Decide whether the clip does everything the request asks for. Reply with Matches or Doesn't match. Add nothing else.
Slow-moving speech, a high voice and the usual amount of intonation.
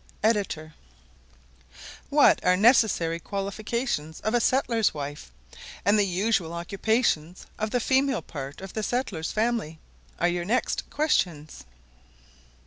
Doesn't match